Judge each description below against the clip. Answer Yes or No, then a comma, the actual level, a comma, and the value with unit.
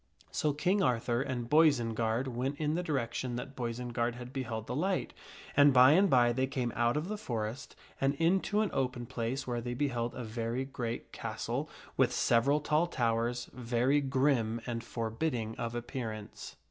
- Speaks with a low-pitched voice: Yes, low, 125 Hz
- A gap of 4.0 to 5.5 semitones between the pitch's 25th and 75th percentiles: No, average, 3.3 semitones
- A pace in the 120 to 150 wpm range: No, average, 170 wpm